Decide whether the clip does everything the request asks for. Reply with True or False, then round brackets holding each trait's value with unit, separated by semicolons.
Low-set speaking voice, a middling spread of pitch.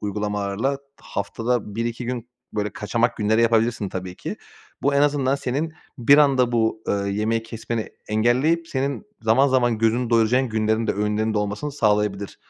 True (115 Hz; 3.3 semitones)